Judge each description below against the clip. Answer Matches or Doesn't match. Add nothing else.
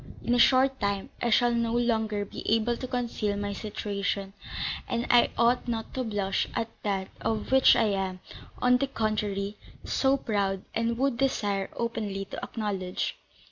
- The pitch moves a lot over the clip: Doesn't match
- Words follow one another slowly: Doesn't match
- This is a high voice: Matches